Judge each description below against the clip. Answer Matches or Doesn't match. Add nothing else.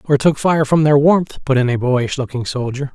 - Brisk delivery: Matches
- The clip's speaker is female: Doesn't match